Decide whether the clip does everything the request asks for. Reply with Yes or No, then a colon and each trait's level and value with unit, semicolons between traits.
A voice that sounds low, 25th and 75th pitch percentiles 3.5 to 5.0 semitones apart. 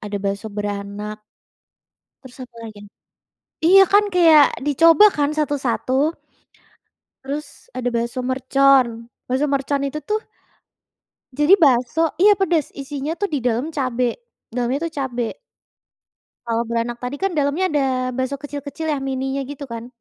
No: very high, 270 Hz; average, 4.0 semitones